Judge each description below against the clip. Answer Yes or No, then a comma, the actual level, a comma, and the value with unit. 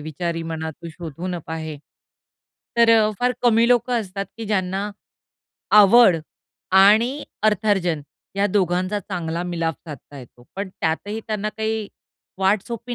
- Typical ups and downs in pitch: Yes, average, 4.6 semitones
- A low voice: No, high, 195 Hz